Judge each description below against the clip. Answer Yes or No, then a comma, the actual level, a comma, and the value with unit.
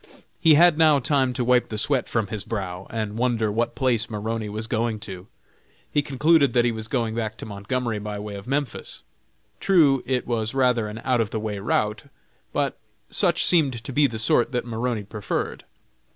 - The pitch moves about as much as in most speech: Yes, average, 3.4 semitones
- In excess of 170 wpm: Yes, average, 195 wpm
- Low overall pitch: Yes, low, 115 Hz